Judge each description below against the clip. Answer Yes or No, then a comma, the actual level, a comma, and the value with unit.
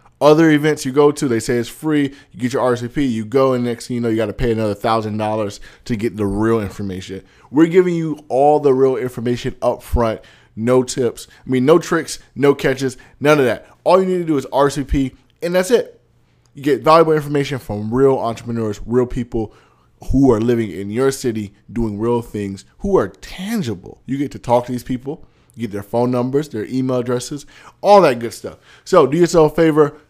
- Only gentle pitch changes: No, average, 4.1 semitones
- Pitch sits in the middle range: No, low, 125 Hz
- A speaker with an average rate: No, fast, 210 wpm